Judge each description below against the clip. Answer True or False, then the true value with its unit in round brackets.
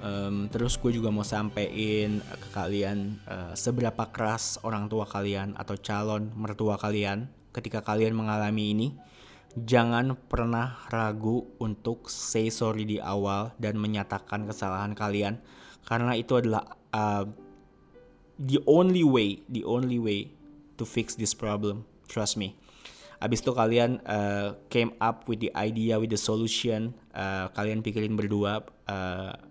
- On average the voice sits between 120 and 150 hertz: False (110 Hz)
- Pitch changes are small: True (2.1 semitones)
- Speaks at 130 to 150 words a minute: True (135 wpm)